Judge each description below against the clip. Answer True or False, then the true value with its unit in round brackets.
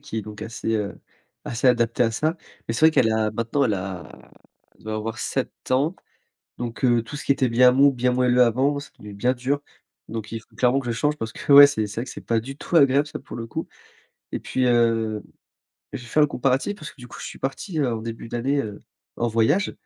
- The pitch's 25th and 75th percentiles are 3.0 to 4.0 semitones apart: True (3.6 semitones)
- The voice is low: True (120 Hz)